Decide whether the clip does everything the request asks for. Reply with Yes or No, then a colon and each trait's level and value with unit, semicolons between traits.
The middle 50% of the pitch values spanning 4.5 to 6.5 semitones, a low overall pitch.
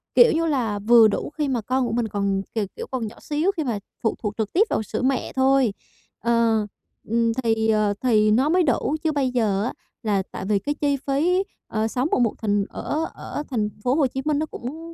No: average, 4.9 semitones; high, 245 Hz